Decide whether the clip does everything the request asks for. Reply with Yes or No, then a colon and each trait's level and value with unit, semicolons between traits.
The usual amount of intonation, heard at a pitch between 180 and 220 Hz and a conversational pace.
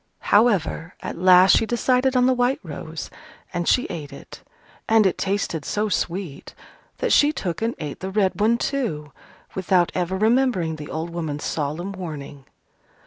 No: wide, 5.7 semitones; medium, 185 Hz; average, 160 wpm